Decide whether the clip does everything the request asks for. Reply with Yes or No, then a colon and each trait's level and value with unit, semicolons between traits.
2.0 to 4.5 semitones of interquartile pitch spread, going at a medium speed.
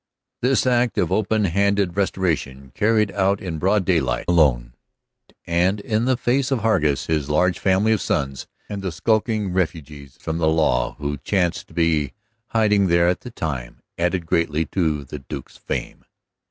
No: average, 5.1 semitones; average, 165 wpm